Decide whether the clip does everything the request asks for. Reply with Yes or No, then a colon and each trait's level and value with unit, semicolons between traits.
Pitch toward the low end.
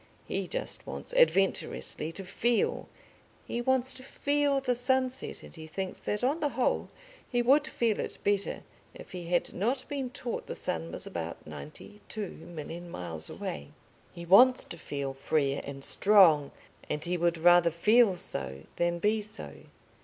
No: high, 190 Hz